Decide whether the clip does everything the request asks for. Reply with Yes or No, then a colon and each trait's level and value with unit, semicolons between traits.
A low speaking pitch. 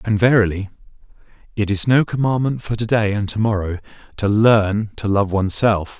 Yes: low, 105 Hz